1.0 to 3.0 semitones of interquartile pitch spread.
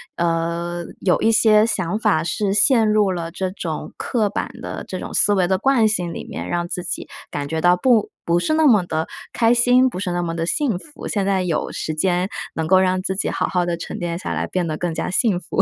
No: average, 3.8 semitones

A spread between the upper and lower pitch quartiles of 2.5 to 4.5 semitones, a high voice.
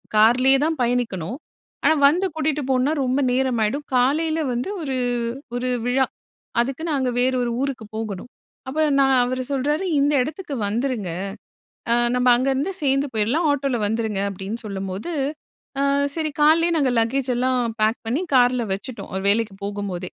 Yes: average, 3.8 semitones; very high, 255 Hz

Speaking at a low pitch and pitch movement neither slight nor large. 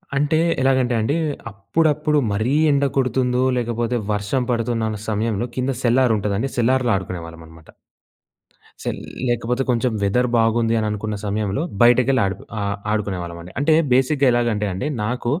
Yes: low, 120 Hz; average, 3.8 semitones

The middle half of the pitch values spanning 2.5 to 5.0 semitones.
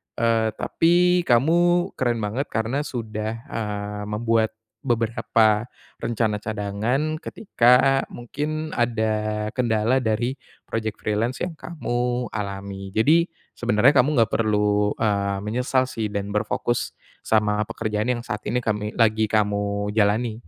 Yes: average, 2.9 semitones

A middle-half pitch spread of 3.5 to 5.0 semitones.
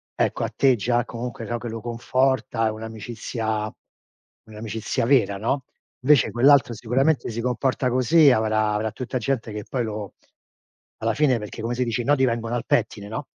No: narrow, 2.6 semitones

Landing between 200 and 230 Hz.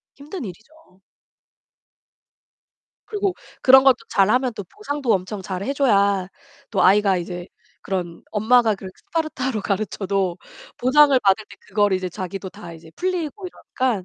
Yes: high, 210 Hz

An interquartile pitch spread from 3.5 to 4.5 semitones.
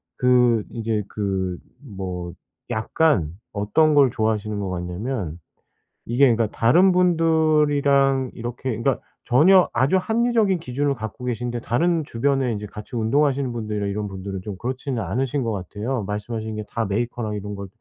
No: average, 5.1 semitones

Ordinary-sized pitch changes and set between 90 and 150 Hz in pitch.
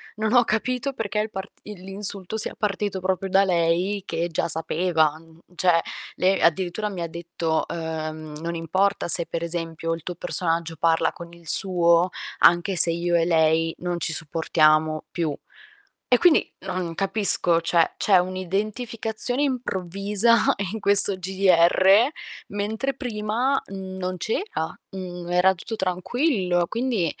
No: average, 3.4 semitones; medium, 185 Hz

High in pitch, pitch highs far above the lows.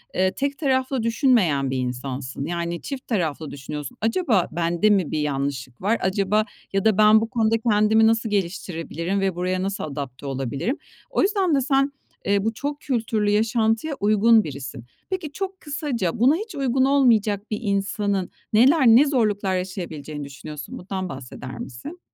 Yes: high, 205 Hz; wide, 6.4 semitones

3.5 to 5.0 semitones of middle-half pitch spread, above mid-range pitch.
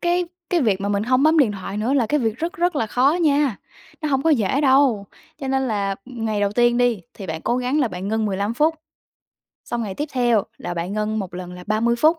No: wide, 5.5 semitones; high, 235 Hz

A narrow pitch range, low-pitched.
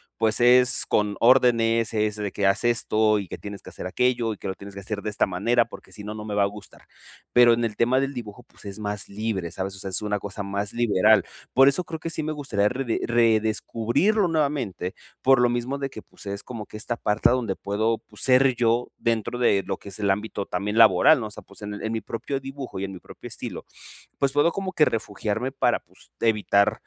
No: average, 3.3 semitones; low, 110 Hz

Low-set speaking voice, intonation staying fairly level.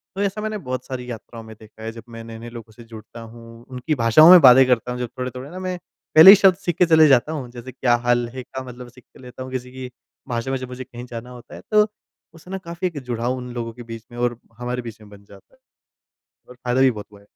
Yes: low, 125 Hz; narrow, 2.2 semitones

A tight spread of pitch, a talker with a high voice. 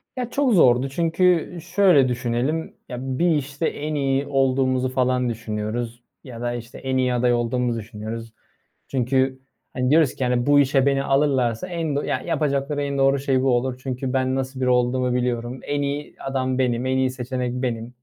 No: narrow, 2.2 semitones; low, 130 Hz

